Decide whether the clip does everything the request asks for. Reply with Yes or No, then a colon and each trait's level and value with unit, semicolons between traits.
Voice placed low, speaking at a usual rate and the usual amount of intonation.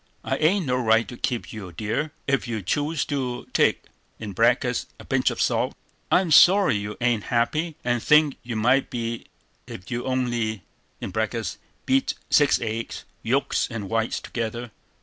Yes: low, 120 Hz; average, 150 wpm; average, 3.8 semitones